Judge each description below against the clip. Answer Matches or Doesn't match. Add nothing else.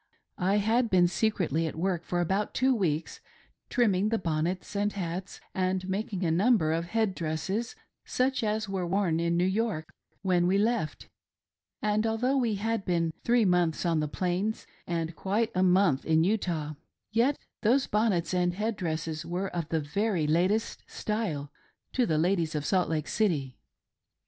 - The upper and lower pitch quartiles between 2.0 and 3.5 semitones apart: Doesn't match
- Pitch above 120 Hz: Matches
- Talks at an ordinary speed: Matches